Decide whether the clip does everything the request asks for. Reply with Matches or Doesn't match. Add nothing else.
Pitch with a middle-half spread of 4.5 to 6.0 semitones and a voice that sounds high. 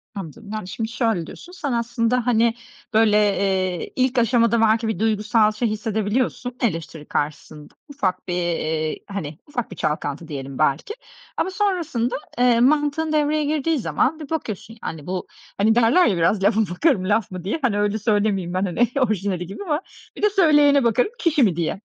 Matches